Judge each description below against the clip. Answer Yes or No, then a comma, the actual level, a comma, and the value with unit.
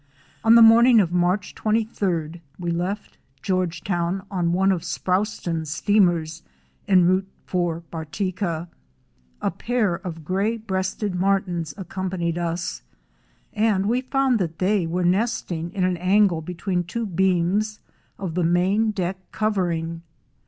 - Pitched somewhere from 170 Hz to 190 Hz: Yes, medium, 185 Hz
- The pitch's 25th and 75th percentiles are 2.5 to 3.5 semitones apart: Yes, average, 3.1 semitones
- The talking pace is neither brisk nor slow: No, slow, 130 wpm